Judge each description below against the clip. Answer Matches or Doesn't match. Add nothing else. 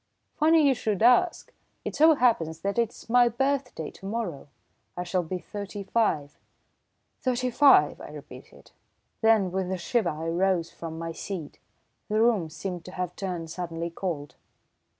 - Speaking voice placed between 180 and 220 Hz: Matches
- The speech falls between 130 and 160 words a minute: Matches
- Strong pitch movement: Matches